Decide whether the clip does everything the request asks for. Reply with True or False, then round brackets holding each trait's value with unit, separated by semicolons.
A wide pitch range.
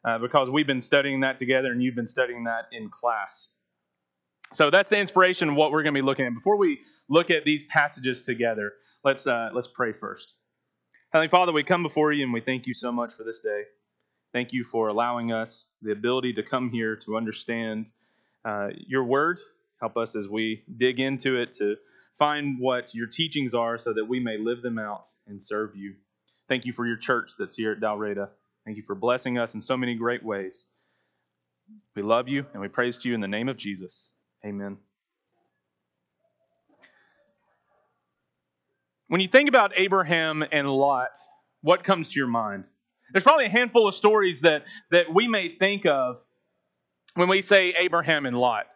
True (6.0 semitones)